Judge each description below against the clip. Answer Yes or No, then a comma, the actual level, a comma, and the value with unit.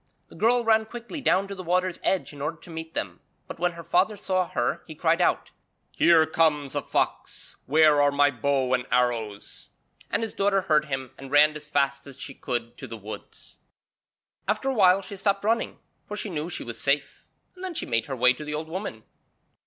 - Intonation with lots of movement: Yes, wide, 6.0 semitones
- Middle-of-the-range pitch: Yes, medium, 155 Hz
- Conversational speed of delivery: No, fast, 215 wpm